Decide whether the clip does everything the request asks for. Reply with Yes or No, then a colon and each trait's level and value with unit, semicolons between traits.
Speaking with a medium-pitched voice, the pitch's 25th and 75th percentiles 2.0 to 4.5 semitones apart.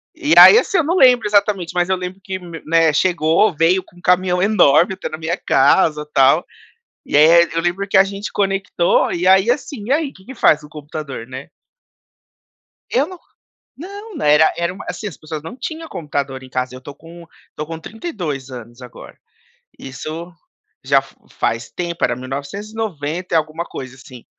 No: medium, 170 Hz; average, 5.1 semitones